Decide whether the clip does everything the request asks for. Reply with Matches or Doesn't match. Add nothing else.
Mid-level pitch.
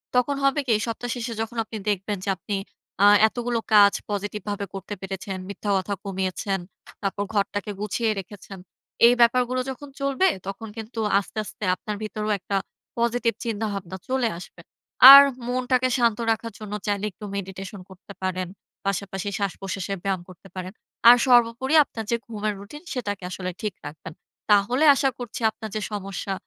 Doesn't match